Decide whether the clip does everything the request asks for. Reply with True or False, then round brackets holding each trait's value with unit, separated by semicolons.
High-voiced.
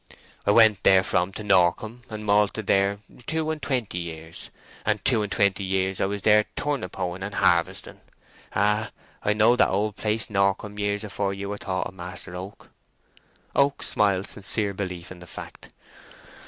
False (100 Hz)